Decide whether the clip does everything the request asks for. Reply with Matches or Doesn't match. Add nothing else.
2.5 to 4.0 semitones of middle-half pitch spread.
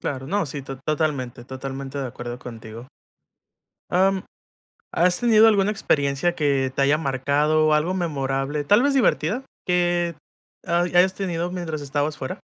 Doesn't match